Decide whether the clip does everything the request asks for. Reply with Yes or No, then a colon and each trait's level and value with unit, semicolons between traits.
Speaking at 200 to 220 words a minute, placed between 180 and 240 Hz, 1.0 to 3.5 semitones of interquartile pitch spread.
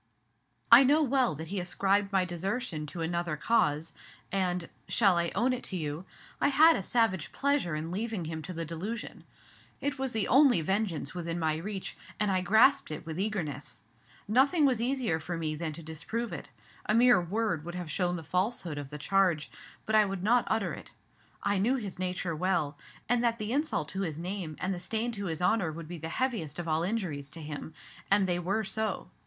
No: fast, 205 wpm; medium, 185 Hz; wide, 5.4 semitones